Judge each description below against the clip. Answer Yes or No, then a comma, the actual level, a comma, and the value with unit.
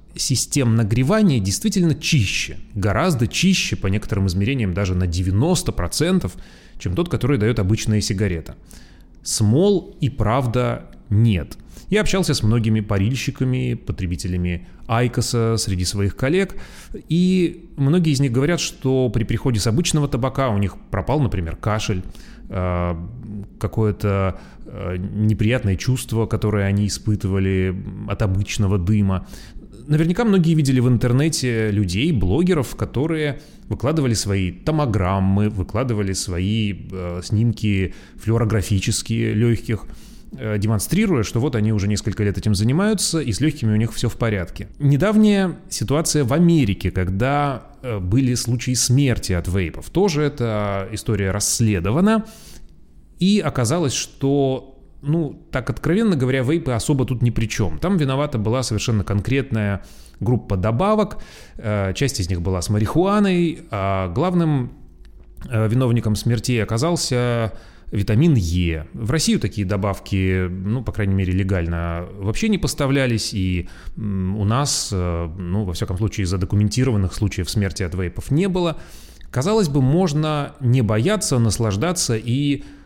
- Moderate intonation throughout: No, wide, 6.1 semitones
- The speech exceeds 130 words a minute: No, average, 125 wpm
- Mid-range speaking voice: No, low, 115 Hz